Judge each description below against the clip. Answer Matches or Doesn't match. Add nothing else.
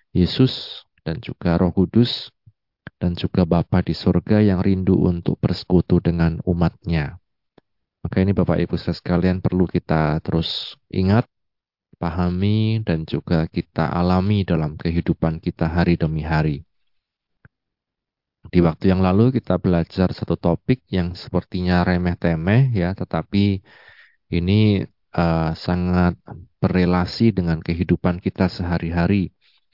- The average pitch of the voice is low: Matches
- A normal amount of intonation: Doesn't match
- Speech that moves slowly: Doesn't match